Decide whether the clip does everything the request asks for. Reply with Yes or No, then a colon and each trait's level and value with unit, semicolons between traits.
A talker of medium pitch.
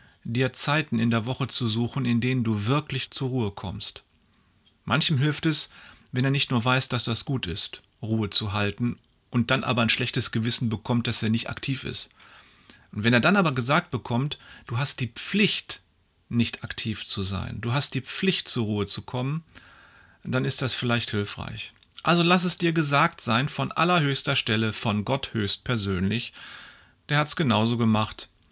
No: low, 120 Hz